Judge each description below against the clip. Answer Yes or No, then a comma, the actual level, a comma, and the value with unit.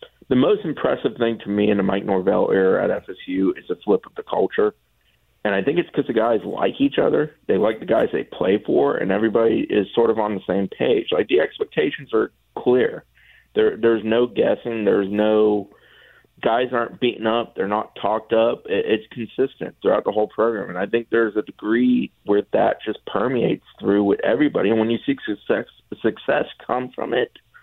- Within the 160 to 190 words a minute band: No, average, 200 wpm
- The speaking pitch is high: No, low, 115 Hz